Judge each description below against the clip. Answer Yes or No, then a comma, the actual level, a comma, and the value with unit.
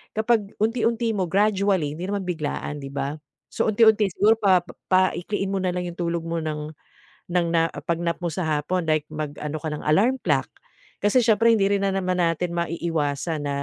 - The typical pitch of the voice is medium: Yes, medium, 175 Hz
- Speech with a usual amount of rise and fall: Yes, average, 4.4 semitones